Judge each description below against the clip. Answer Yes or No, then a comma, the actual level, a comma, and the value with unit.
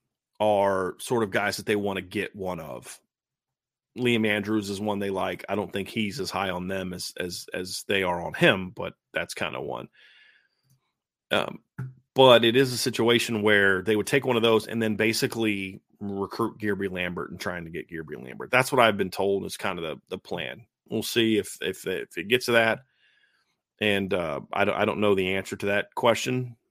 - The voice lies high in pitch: No, low, 105 Hz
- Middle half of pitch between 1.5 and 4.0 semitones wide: Yes, average, 2.9 semitones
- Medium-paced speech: No, fast, 210 wpm